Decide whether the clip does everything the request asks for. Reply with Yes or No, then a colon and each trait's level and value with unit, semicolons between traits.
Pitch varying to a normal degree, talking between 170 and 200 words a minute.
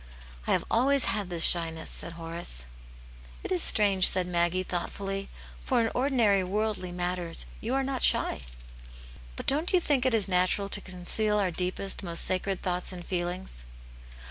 Yes: average, 3.5 semitones; average, 175 wpm